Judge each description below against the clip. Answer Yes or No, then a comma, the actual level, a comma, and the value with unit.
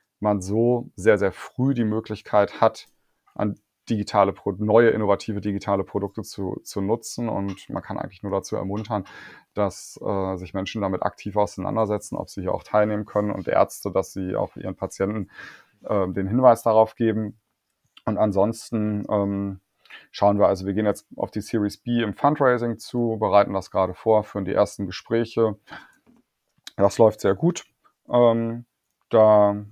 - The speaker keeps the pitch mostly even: Yes, narrow, 2.1 semitones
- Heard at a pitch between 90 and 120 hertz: Yes, low, 105 Hz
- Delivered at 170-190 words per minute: No, average, 160 wpm